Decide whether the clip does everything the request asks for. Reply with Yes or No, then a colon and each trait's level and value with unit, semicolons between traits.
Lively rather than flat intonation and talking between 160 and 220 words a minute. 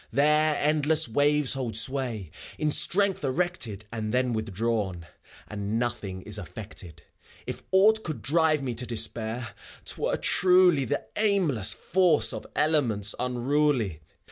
No: wide, 5.7 semitones; slow, 135 wpm